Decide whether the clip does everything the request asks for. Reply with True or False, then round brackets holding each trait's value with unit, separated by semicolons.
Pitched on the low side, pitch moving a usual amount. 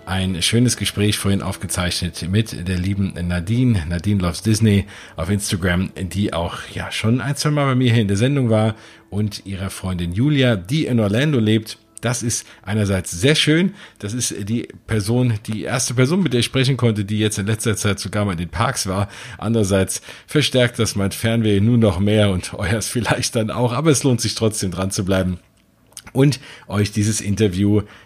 True (110 Hz; 3.5 semitones)